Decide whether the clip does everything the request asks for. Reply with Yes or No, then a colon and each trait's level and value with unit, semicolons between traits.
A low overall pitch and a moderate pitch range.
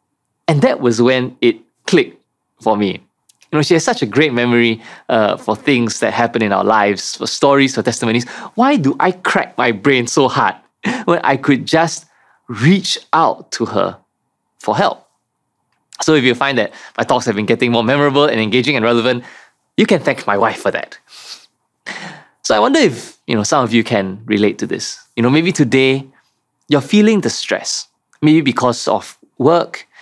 Yes: low, 125 Hz; average, 3.7 semitones